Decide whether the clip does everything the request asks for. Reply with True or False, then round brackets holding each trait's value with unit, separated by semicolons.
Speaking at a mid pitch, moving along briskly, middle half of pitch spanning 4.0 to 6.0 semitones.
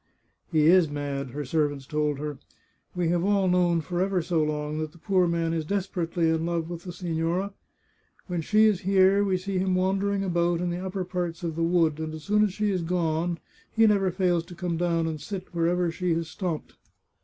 False (175 Hz; 225 wpm; 2.4 semitones)